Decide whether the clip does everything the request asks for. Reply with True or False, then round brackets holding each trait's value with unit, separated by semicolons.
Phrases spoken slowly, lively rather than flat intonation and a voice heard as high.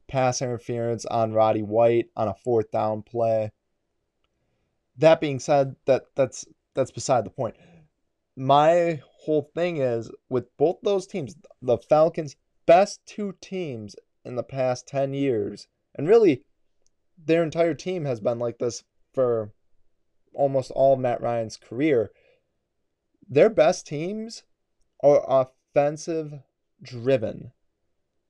False (125 wpm; 5.8 semitones; 135 Hz)